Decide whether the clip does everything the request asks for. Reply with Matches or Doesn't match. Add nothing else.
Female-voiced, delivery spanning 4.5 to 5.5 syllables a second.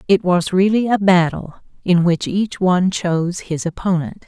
Matches